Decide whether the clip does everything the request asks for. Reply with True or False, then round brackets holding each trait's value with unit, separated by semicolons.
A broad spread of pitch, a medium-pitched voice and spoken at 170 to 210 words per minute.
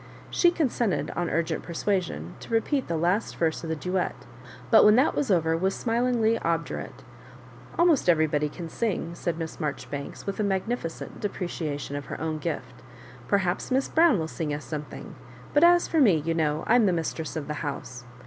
True (6.3 semitones; 170 Hz; 190 wpm)